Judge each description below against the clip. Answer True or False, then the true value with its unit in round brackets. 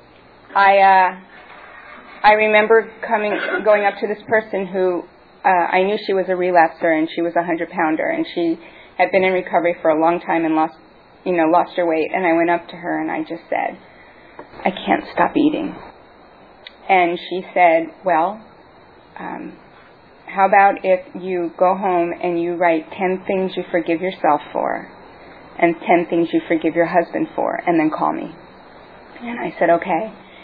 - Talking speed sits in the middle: True (180 wpm)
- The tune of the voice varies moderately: True (3.1 semitones)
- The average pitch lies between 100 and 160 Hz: False (180 Hz)